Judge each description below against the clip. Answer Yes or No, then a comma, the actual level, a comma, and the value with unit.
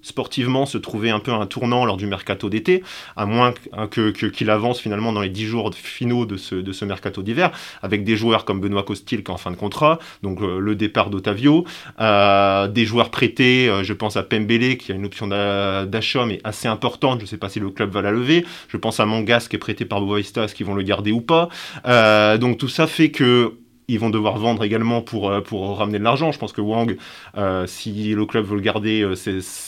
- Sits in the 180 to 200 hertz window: No, low, 110 Hz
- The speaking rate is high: Yes, fast, 240 wpm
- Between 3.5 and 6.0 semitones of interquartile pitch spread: No, average, 3.0 semitones